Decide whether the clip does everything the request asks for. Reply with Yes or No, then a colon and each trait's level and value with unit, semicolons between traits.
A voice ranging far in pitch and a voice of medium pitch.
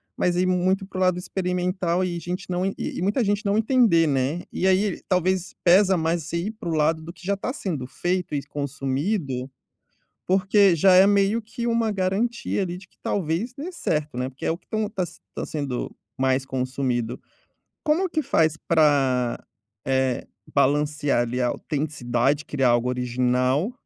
Yes: wide, 5.9 semitones; medium, 170 Hz